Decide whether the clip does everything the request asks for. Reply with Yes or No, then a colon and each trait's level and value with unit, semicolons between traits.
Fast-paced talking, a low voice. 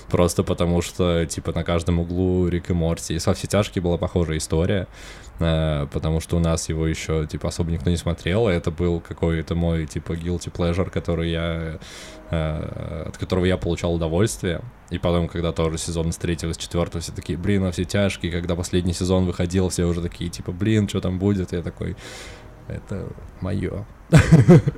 Yes: fast, 185 wpm; very low, 90 Hz